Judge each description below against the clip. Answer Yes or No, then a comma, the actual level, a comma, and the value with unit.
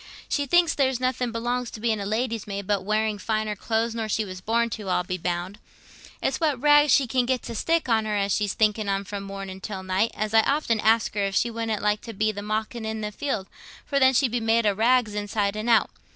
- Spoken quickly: Yes, fast, 245 wpm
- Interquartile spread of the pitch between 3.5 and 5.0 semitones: No, average, 2.8 semitones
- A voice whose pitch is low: No, high, 220 Hz